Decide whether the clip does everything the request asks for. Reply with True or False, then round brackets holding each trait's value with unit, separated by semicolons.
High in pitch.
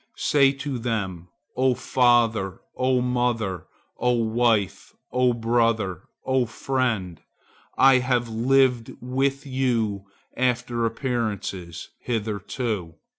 False (120 Hz)